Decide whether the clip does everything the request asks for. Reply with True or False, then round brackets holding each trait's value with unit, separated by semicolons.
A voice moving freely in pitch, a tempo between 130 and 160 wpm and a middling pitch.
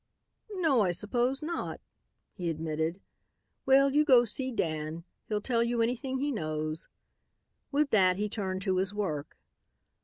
False (7.5 semitones; 145 wpm; 210 Hz)